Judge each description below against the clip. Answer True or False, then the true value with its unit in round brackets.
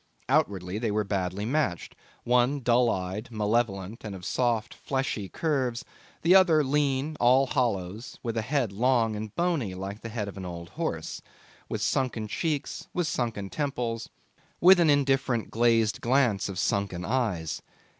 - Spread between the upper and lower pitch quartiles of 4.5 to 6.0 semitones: True (4.9 semitones)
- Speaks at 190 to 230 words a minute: False (155 wpm)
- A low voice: True (115 Hz)